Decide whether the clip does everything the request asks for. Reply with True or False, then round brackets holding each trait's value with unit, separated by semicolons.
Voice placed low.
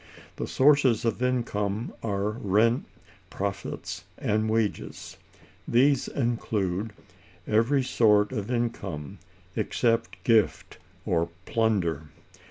True (110 Hz)